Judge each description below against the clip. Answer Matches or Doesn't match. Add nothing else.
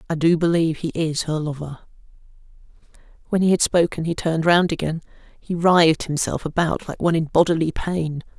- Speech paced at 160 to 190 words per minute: Matches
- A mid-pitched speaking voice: Matches